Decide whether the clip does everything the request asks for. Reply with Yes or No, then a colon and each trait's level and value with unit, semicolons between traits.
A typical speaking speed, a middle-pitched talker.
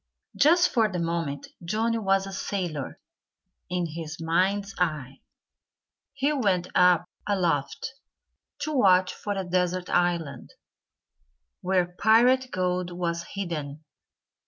No: slow, 110 wpm; medium, 180 Hz